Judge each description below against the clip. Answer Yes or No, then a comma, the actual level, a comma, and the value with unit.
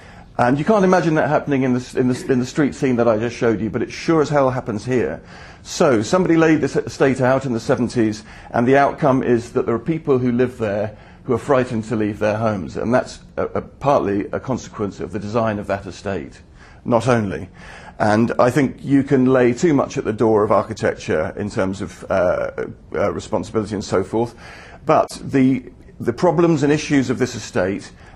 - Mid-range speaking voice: No, low, 125 Hz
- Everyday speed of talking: No, fast, 210 wpm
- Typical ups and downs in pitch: Yes, average, 4.4 semitones